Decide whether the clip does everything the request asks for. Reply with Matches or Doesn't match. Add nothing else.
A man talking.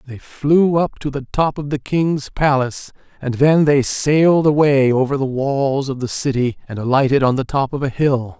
Matches